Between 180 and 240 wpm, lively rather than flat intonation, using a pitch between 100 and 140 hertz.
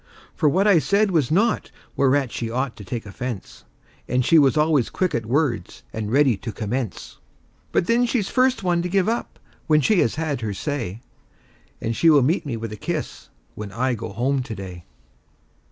Yes: average, 195 wpm; wide, 6.6 semitones; low, 135 Hz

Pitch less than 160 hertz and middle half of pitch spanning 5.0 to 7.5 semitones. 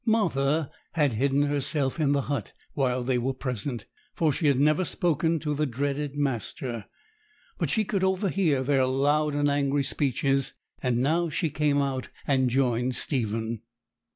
No: medium, 140 Hz; average, 2.7 semitones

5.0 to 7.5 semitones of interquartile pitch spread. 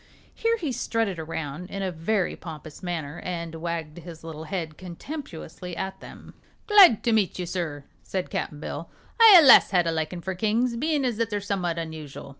Yes: average, 5.3 semitones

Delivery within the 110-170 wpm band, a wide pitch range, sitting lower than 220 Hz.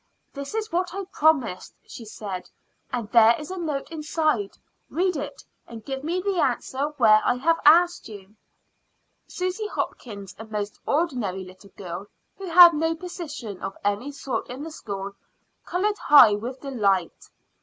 No: average, 155 wpm; wide, 8.0 semitones; very high, 275 Hz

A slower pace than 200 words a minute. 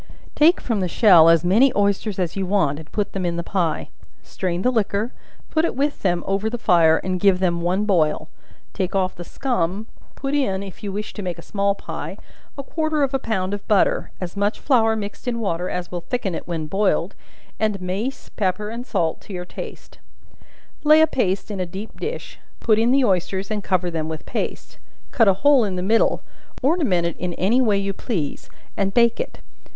No: fast, 205 wpm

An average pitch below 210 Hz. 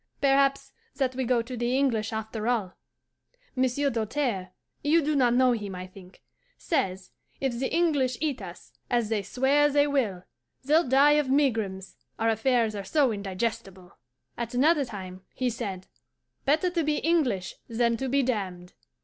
No: high, 245 Hz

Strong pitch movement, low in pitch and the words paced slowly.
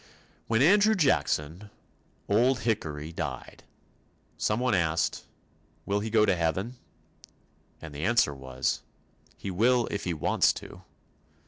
Yes: wide, 6.8 semitones; low, 100 Hz; slow, 120 wpm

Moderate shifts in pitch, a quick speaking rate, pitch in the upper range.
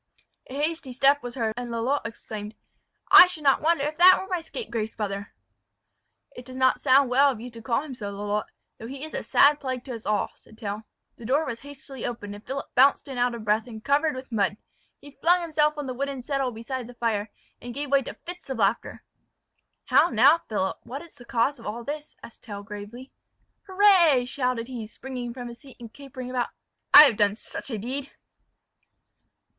Yes: average, 3.8 semitones; fast, 210 wpm; very high, 255 Hz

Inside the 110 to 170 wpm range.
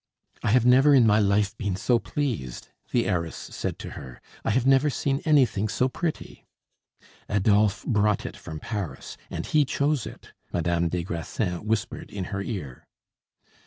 Yes: average, 160 wpm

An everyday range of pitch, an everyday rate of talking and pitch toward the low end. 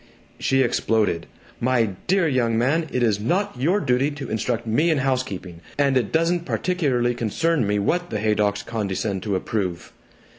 No: wide, 5.9 semitones; average, 160 wpm; low, 120 Hz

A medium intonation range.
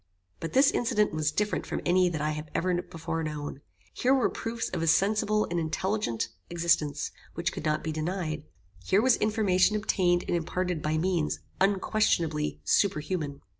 Yes: average, 4.6 semitones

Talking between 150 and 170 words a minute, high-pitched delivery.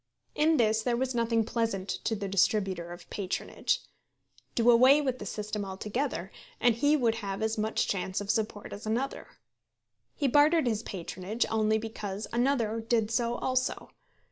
Yes: average, 160 wpm; high, 225 Hz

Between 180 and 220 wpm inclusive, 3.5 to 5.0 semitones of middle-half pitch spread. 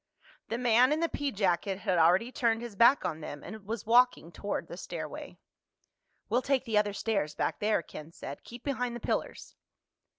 Yes: average, 190 wpm; average, 4.4 semitones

